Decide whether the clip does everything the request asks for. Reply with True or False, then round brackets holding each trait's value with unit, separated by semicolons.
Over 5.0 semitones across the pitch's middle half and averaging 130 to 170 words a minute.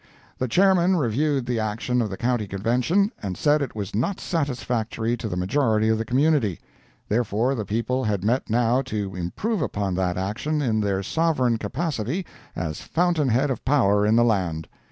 False (5.5 semitones; 180 wpm)